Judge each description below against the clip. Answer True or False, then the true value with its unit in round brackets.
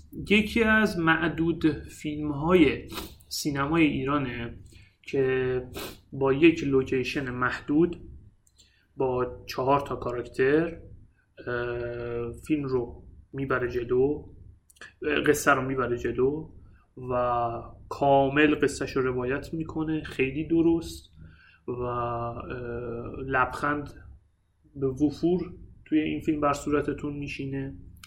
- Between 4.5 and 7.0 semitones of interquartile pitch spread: False (3.9 semitones)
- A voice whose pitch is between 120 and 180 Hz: True (135 Hz)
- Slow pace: True (90 wpm)